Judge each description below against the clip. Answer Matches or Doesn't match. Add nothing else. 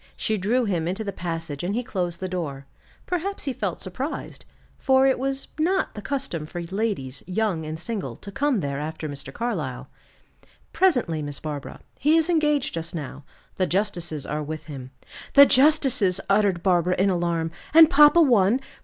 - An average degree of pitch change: Doesn't match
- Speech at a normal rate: Matches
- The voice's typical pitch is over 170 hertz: Matches